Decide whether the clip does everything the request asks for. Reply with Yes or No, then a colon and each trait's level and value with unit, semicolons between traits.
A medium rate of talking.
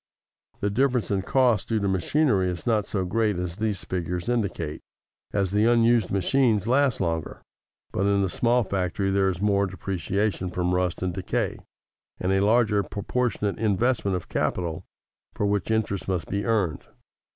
Yes: average, 165 wpm